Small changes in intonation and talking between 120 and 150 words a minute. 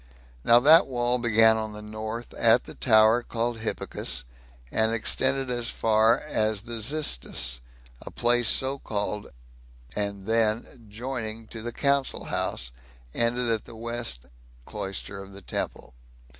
Yes: narrow, 2.0 semitones; average, 140 wpm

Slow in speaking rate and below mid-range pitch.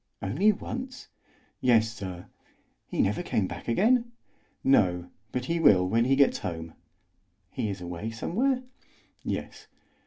Yes: slow, 130 wpm; low, 115 Hz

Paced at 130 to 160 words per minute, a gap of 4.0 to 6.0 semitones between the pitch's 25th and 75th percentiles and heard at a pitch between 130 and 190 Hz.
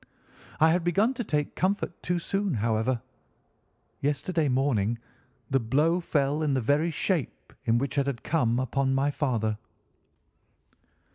Yes: average, 140 wpm; average, 4.7 semitones; medium, 140 Hz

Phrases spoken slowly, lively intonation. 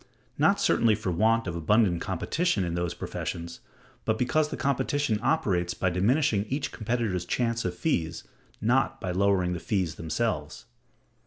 No: average, 150 wpm; wide, 5.7 semitones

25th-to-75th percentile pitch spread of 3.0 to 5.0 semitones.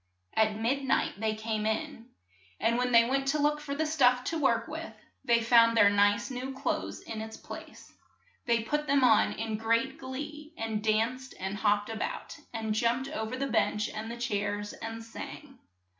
Yes: average, 3.5 semitones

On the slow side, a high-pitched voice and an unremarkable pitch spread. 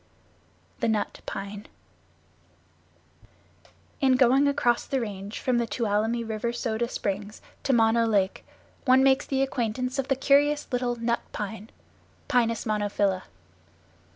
Yes: slow, 125 wpm; high, 235 Hz; average, 3.4 semitones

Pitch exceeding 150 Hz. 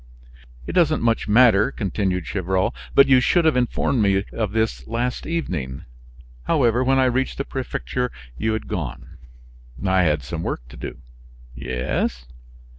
No: low, 110 Hz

